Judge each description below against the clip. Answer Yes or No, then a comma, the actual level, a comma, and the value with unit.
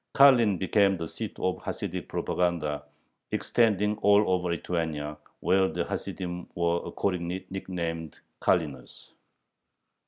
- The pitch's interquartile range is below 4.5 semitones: Yes, average, 2.9 semitones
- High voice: No, very low, 90 Hz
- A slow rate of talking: Yes, slow, 115 wpm